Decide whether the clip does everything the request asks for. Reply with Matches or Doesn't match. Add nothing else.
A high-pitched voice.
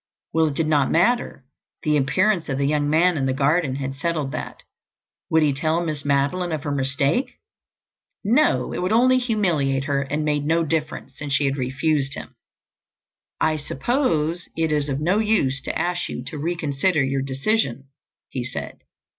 Doesn't match